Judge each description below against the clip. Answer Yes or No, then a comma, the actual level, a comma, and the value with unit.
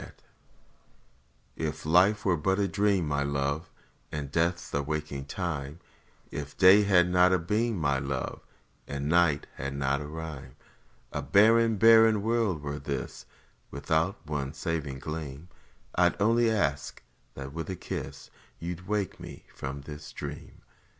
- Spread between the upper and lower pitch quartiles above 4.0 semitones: Yes, average, 5.1 semitones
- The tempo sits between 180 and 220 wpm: No, average, 150 wpm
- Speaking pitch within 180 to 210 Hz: No, very low, 80 Hz